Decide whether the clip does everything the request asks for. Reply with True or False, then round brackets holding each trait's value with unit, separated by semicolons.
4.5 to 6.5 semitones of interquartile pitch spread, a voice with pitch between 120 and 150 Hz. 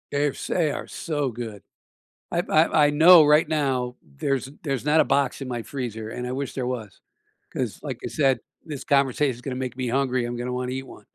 False (2.8 semitones; 135 Hz)